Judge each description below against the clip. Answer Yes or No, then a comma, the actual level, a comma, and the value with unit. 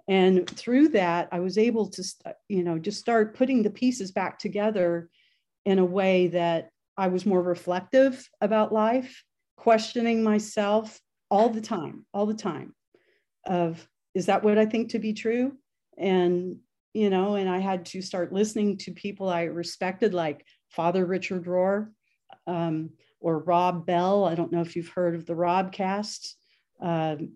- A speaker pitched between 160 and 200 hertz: Yes, high, 190 Hz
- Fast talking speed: No, average, 165 wpm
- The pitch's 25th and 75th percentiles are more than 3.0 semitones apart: Yes, average, 3.4 semitones